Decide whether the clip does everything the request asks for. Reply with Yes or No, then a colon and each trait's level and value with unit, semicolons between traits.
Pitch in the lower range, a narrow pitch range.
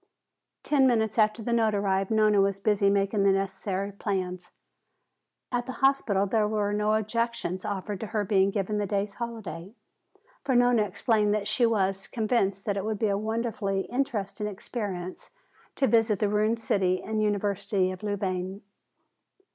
No: high, 205 Hz; narrow, 2.0 semitones